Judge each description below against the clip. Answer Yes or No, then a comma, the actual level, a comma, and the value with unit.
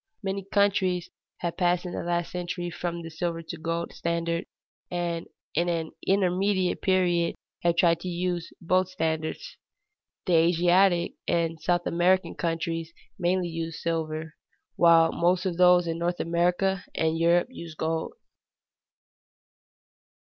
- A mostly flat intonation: Yes, narrow, 1.4 semitones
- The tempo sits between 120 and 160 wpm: Yes, slow, 135 wpm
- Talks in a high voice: No, medium, 175 Hz